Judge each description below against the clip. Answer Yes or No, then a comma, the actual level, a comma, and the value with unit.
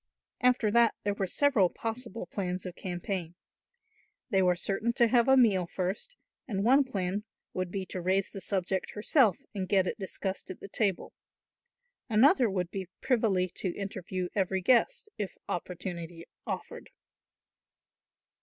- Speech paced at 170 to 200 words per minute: No, average, 145 wpm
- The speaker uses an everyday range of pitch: Yes, average, 3.7 semitones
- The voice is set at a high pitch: Yes, high, 195 Hz